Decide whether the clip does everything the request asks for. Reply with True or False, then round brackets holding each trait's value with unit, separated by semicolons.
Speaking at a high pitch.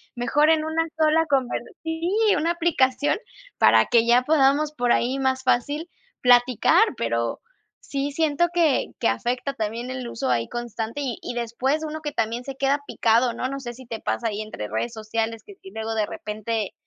True (255 Hz)